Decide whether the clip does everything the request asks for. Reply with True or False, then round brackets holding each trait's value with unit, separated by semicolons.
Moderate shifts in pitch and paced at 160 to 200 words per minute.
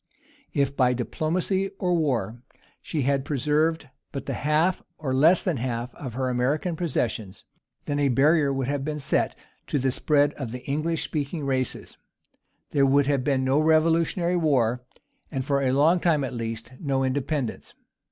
True (3.2 semitones; 170 wpm)